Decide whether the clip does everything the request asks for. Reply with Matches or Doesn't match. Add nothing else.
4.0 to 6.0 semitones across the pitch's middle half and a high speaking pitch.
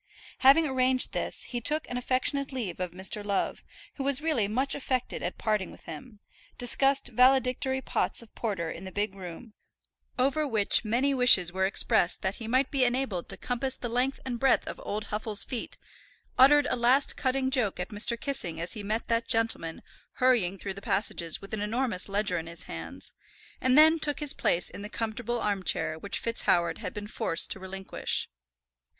Matches